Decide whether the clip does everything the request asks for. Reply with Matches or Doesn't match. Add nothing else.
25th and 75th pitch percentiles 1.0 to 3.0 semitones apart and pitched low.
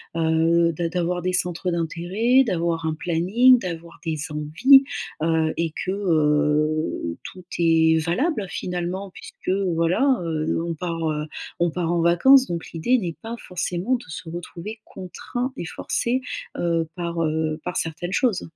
Doesn't match